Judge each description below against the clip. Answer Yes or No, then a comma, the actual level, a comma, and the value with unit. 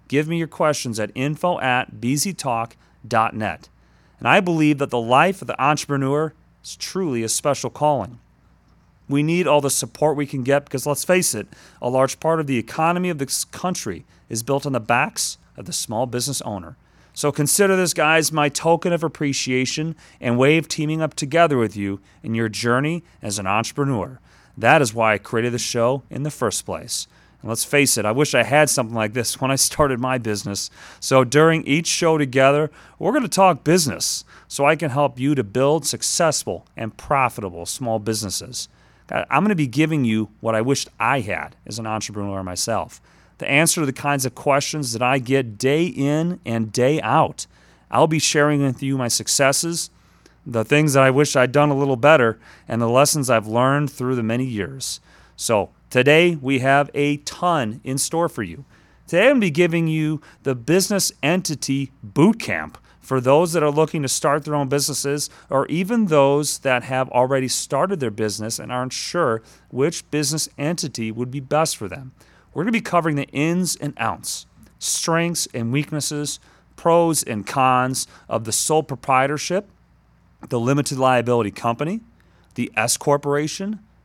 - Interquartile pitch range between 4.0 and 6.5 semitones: Yes, average, 4.3 semitones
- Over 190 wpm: No, average, 185 wpm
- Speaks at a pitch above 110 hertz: Yes, low, 135 Hz